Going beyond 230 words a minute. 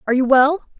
No: fast, 225 wpm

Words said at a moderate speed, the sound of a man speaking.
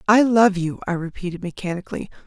No: average, 160 wpm; female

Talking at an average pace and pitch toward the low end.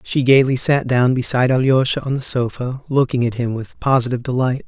Yes: average, 195 wpm; low, 125 Hz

